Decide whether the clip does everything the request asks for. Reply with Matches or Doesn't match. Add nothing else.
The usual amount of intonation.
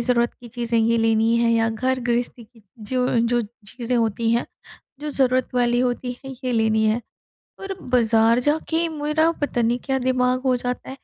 Doesn't match